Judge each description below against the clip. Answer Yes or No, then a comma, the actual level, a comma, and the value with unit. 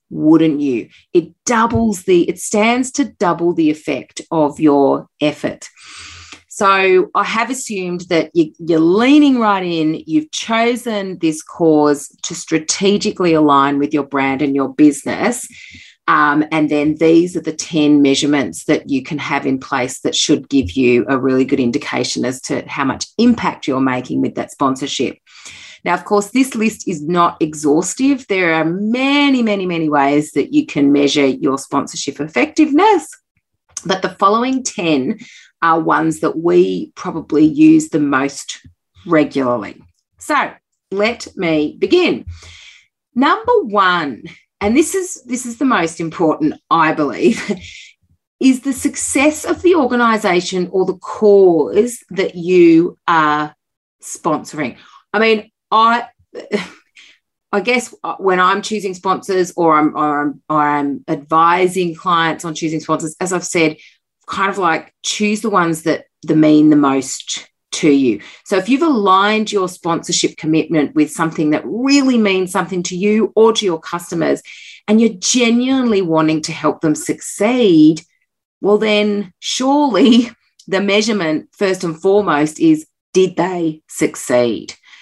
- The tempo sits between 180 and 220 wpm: No, average, 145 wpm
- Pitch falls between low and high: Yes, medium, 180 Hz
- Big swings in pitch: Yes, wide, 6.6 semitones